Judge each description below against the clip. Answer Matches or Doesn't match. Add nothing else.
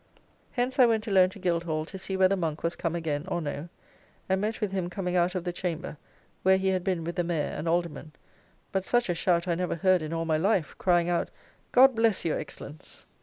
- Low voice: Doesn't match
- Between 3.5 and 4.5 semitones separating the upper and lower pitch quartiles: Doesn't match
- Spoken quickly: Matches